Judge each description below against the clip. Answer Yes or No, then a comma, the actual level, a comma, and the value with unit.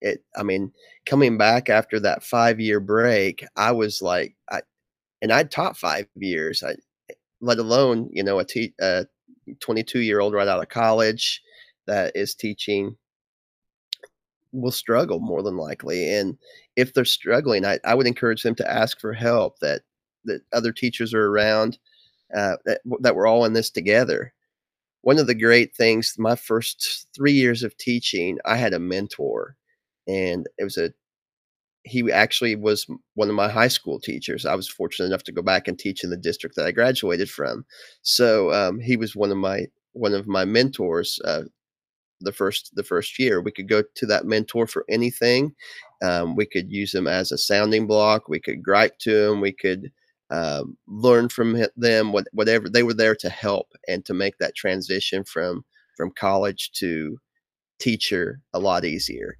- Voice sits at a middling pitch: No, low, 115 Hz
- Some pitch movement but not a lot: Yes, average, 3.0 semitones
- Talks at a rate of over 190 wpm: No, average, 175 wpm